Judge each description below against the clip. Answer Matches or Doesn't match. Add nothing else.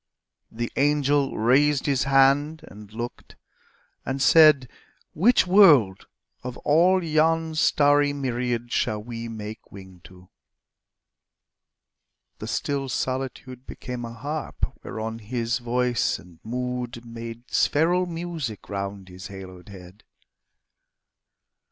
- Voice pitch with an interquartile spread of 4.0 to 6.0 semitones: Matches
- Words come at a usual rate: Doesn't match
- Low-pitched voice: Matches